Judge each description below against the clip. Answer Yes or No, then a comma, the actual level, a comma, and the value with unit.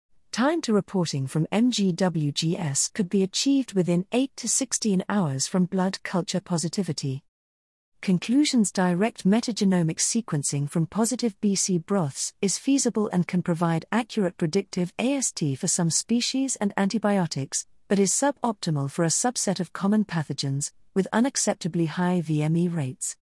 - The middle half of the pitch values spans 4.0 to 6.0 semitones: Yes, average, 4.6 semitones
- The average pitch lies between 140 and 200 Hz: Yes, medium, 185 Hz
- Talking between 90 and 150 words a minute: Yes, slow, 135 wpm